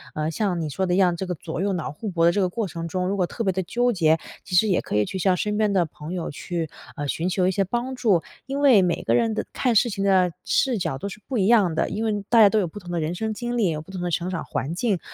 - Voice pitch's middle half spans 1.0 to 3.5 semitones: No, average, 3.9 semitones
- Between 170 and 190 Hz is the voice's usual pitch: Yes, medium, 185 Hz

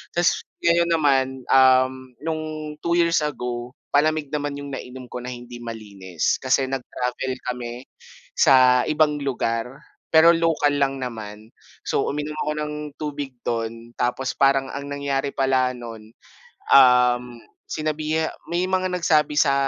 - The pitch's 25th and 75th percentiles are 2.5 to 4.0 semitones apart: Yes, average, 3.6 semitones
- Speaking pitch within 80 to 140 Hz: Yes, low, 135 Hz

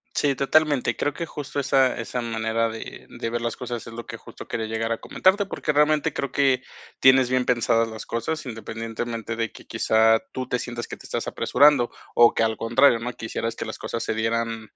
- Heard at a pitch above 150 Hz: No, low, 120 Hz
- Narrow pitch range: No, average, 3.1 semitones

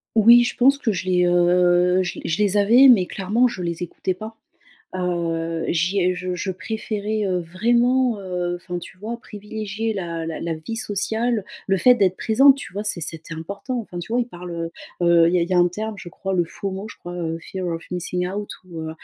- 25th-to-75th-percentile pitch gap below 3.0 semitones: No, average, 3.8 semitones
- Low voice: No, medium, 185 Hz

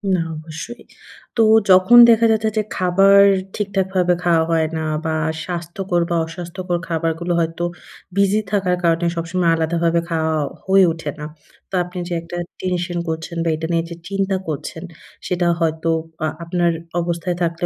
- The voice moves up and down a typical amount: No, narrow, 2.0 semitones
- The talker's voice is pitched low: No, medium, 175 Hz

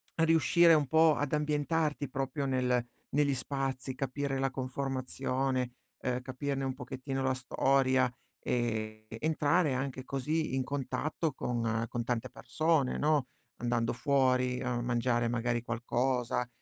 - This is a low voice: Yes, low, 130 Hz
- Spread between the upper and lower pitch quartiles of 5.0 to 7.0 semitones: No, narrow, 2.4 semitones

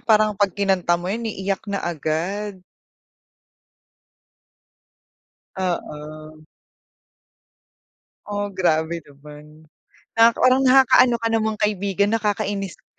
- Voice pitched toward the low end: No, high, 195 Hz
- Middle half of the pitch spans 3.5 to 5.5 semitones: Yes, average, 4.1 semitones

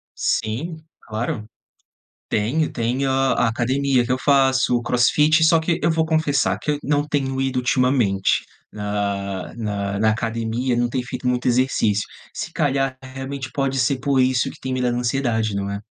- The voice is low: Yes, low, 125 Hz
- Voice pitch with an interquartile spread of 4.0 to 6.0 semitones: No, average, 3.3 semitones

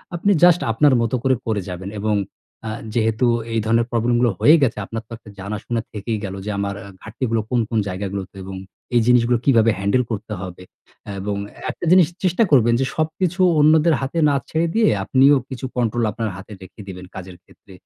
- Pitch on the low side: Yes, low, 115 Hz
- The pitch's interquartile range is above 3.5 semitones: Yes, average, 5.1 semitones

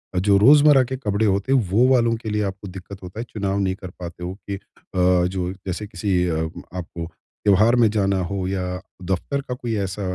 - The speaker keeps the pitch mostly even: No, average, 3.2 semitones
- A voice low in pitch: Yes, low, 100 Hz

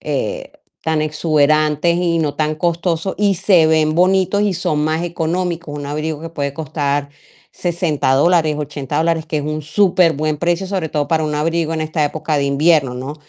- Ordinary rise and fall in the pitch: No, narrow, 2.3 semitones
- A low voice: No, medium, 160 Hz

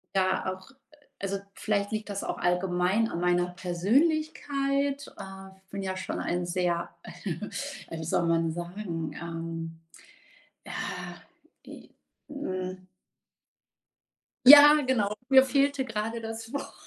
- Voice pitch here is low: No, high, 190 Hz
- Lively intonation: Yes, wide, 5.8 semitones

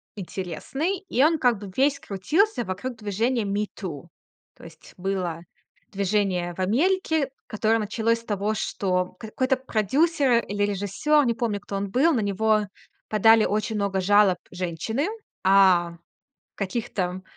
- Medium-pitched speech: No, high, 210 Hz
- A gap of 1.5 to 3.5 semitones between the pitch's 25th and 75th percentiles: No, average, 4.3 semitones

